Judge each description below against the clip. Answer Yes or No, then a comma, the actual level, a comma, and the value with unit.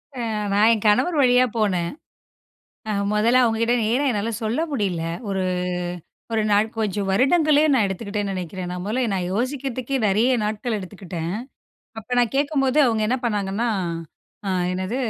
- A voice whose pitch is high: Yes, high, 220 Hz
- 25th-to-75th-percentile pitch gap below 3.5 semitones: No, average, 4.3 semitones